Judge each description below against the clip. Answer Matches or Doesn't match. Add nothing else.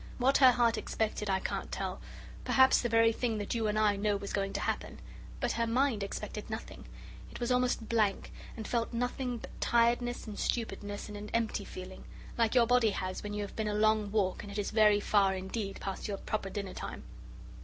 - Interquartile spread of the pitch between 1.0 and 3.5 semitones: Matches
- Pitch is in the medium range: Doesn't match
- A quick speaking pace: Matches